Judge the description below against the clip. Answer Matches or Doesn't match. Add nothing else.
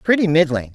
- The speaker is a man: Doesn't match